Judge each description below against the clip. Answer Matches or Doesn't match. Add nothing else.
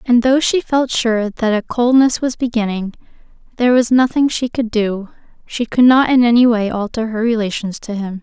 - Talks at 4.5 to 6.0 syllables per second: Matches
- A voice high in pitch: Matches